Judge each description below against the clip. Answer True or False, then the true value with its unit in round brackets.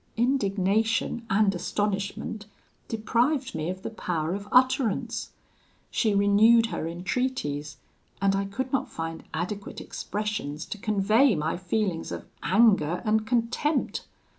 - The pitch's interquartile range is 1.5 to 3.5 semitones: False (4.0 semitones)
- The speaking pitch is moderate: False (210 Hz)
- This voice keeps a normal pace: False (120 wpm)